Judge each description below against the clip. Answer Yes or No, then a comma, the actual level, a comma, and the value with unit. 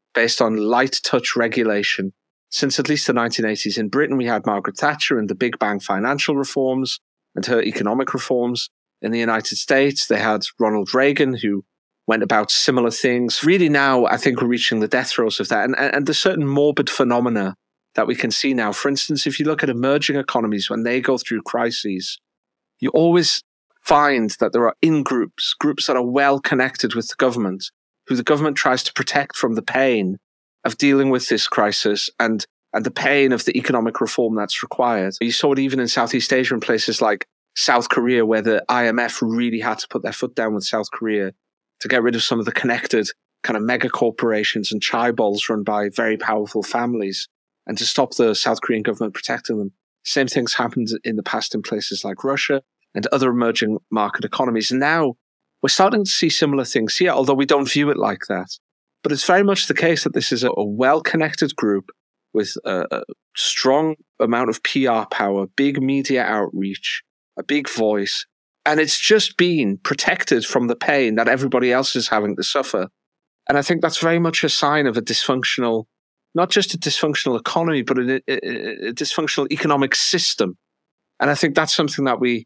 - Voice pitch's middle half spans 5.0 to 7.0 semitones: No, average, 4.1 semitones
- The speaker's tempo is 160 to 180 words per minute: No, average, 195 wpm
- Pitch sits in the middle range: No, low, 130 Hz